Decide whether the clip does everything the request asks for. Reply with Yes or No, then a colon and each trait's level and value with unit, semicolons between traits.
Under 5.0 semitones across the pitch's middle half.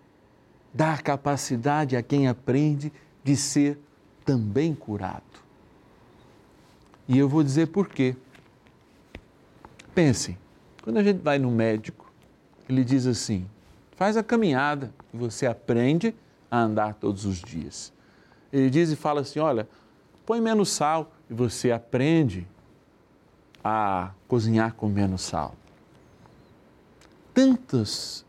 No: wide, 5.4 semitones